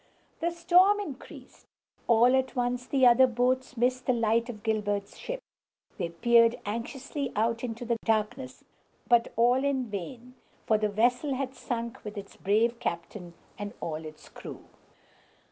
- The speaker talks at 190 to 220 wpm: No, average, 150 wpm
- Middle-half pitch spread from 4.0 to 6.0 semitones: No, average, 3.1 semitones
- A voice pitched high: Yes, high, 235 Hz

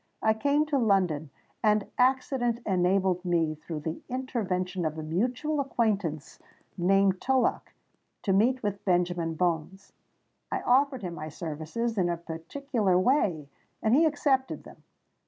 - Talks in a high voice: Yes, high, 195 Hz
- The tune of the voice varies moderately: No, wide, 6.5 semitones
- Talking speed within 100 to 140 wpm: Yes, slow, 135 wpm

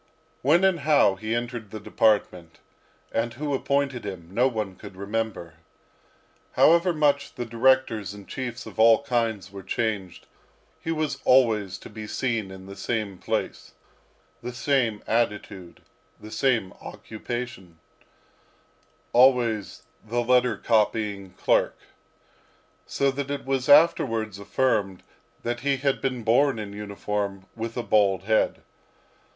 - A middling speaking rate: No, slow, 130 wpm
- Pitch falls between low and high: No, low, 115 Hz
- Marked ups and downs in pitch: No, average, 4.3 semitones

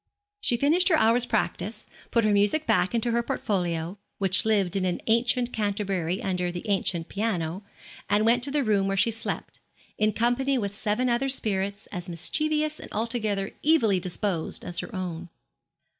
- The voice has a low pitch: No, high, 210 Hz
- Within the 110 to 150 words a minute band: No, average, 170 wpm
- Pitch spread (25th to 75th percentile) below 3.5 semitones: No, average, 4.1 semitones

